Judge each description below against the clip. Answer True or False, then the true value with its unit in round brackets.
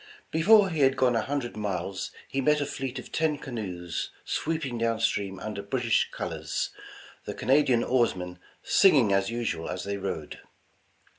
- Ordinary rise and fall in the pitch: False (5.7 semitones)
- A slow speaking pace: False (160 wpm)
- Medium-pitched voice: False (120 Hz)